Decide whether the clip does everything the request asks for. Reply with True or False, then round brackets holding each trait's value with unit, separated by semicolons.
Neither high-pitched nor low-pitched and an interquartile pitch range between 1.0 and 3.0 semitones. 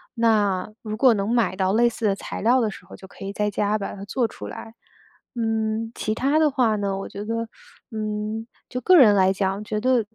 False (215 Hz; 2.5 semitones)